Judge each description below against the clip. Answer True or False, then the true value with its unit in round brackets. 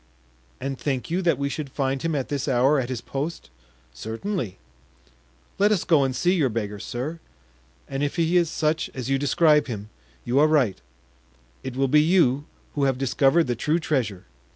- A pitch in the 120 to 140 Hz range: True (135 Hz)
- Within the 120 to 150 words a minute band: False (180 wpm)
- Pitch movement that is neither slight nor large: True (4.3 semitones)